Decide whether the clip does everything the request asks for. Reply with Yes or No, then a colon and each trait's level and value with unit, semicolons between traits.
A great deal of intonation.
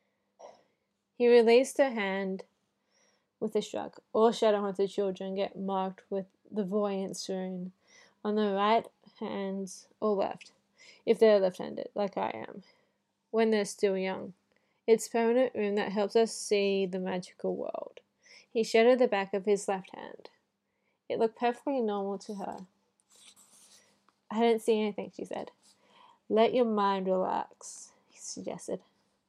No: average, 2.8 semitones